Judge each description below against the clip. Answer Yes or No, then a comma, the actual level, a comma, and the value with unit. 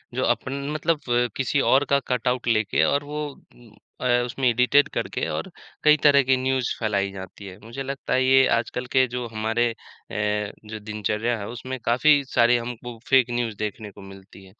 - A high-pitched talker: No, low, 120 Hz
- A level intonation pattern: No, average, 3.3 semitones